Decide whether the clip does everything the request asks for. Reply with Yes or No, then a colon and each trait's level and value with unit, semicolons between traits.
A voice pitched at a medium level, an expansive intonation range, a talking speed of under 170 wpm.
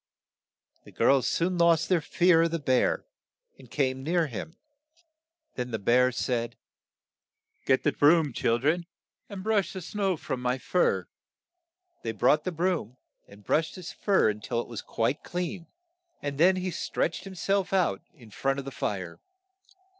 Yes: medium, 155 Hz; wide, 6.1 semitones; average, 160 wpm